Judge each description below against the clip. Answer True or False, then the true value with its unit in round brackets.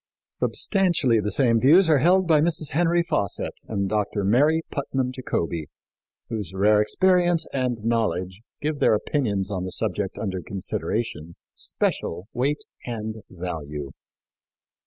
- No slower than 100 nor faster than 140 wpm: True (135 wpm)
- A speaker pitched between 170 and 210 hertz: False (115 Hz)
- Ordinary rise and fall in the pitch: False (7.6 semitones)